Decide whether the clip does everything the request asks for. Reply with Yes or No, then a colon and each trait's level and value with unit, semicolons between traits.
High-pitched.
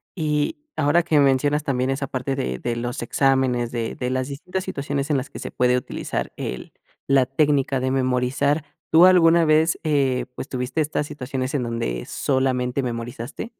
No: low, 135 Hz